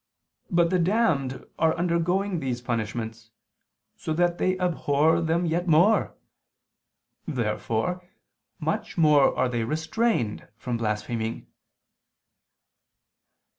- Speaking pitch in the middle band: Yes, medium, 160 Hz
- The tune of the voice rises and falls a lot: Yes, wide, 6.7 semitones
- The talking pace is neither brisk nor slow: No, slow, 95 wpm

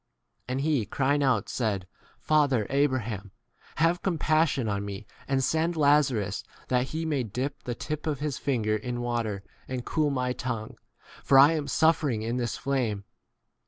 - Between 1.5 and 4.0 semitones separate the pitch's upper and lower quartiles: No, average, 4.4 semitones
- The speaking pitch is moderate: No, low, 130 Hz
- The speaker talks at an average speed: Yes, average, 165 wpm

